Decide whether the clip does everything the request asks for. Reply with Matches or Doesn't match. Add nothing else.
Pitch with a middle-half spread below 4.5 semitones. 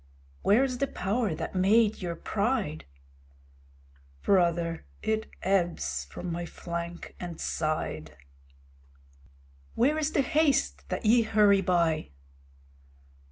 Doesn't match